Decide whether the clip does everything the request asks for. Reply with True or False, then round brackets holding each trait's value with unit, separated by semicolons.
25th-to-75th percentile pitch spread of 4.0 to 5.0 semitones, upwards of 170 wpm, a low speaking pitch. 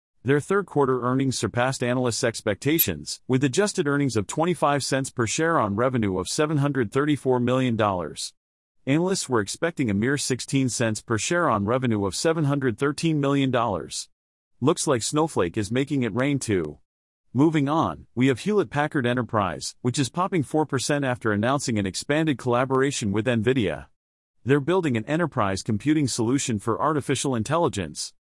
False (4.5 semitones; 145 wpm; 130 Hz)